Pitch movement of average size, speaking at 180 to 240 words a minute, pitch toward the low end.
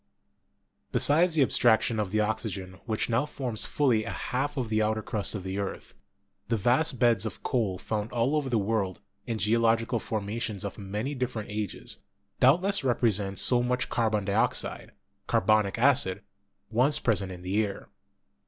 No: average, 3.2 semitones; average, 170 wpm; low, 110 Hz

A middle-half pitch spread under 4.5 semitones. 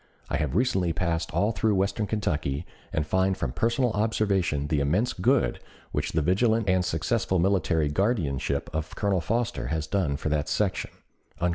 No: average, 5.3 semitones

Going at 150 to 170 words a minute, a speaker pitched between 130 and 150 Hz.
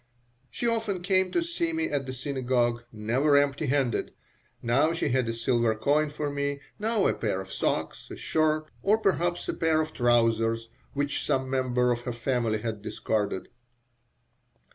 Yes: average, 165 wpm; low, 135 Hz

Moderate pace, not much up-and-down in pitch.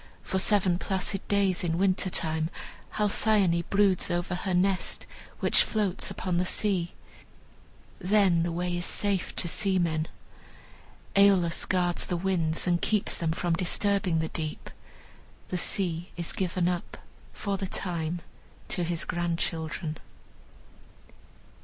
No: slow, 130 wpm; narrow, 2.3 semitones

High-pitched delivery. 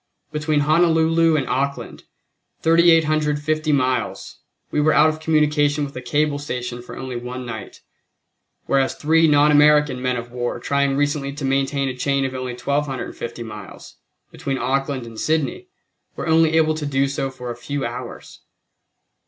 No: medium, 140 Hz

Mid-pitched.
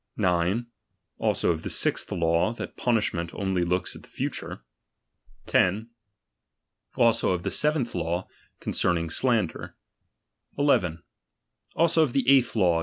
No: very low, 95 Hz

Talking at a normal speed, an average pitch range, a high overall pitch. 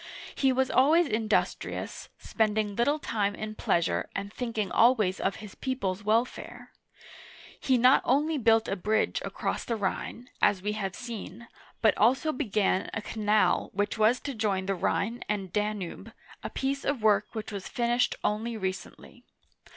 Yes: average, 165 wpm; average, 3.3 semitones; high, 215 Hz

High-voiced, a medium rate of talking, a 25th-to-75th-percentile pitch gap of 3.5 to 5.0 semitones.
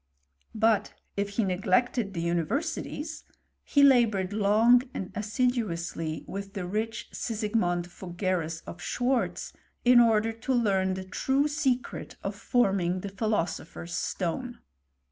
No: high, 205 Hz; slow, 125 wpm; average, 4.6 semitones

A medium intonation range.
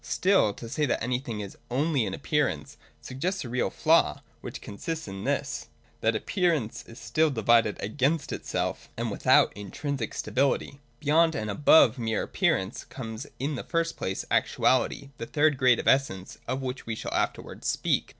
Yes: average, 4.7 semitones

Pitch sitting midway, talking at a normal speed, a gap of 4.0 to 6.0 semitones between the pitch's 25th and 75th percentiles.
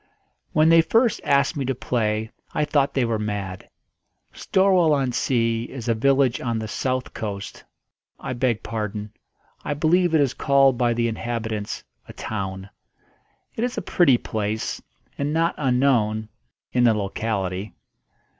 No: low, 120 Hz; average, 150 wpm; average, 4.4 semitones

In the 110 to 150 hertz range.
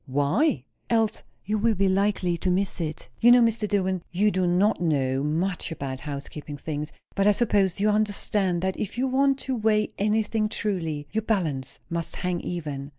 No: high, 190 Hz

